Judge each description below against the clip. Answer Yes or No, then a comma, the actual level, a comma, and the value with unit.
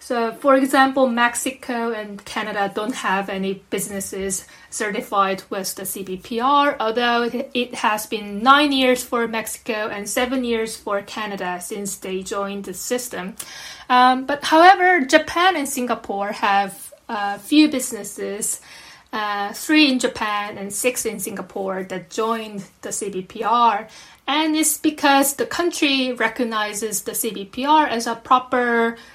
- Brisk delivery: No, slow, 135 wpm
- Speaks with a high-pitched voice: Yes, high, 230 Hz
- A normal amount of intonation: Yes, average, 4.3 semitones